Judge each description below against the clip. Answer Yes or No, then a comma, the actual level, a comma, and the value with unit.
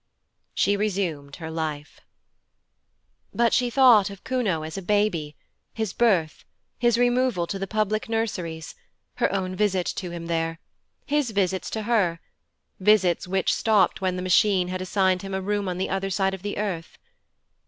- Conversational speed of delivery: Yes, average, 165 wpm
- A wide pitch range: No, average, 3.3 semitones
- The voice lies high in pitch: Yes, high, 195 Hz